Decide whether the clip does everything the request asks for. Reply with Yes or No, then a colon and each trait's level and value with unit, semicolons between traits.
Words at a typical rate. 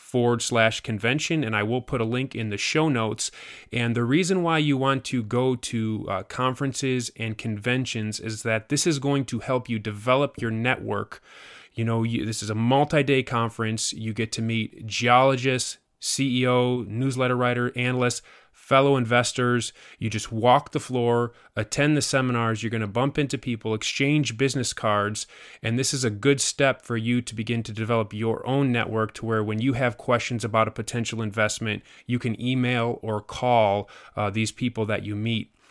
Yes: average, 180 wpm